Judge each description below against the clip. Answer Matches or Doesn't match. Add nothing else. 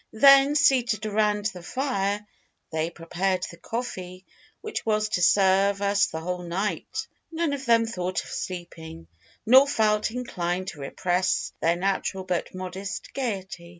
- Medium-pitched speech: Doesn't match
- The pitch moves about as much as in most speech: Matches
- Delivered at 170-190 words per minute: Doesn't match